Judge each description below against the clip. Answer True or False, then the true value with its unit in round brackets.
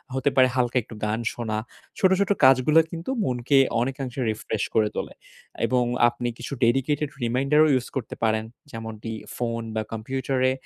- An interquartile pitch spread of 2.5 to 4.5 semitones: True (2.9 semitones)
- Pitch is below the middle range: True (125 Hz)